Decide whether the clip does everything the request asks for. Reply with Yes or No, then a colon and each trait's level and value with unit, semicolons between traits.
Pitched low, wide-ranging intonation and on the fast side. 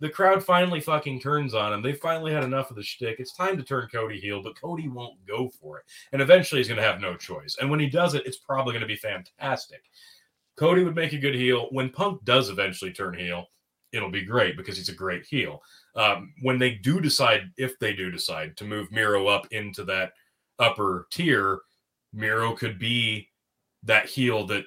Yes: low, 125 Hz; wide, 6.3 semitones; fast, 215 wpm